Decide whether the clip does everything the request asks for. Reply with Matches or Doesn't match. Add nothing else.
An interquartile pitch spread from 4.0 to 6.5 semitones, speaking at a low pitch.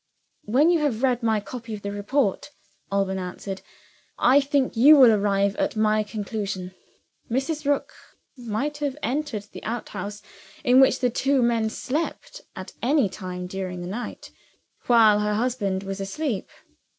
Doesn't match